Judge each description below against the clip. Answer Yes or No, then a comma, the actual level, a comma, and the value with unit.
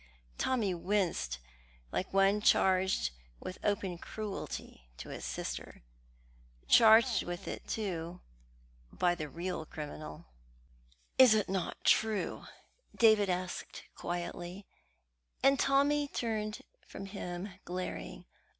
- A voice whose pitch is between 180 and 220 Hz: Yes, high, 190 Hz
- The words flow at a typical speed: No, slow, 105 wpm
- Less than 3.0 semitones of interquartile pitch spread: No, average, 3.6 semitones